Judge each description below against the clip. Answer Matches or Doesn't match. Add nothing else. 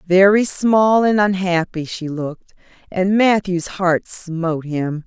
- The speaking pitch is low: Doesn't match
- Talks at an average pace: Doesn't match